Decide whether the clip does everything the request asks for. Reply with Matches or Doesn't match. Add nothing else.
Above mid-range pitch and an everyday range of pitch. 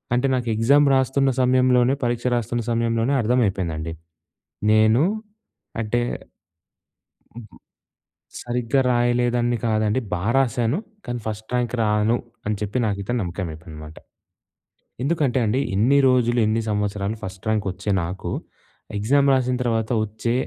Doesn't match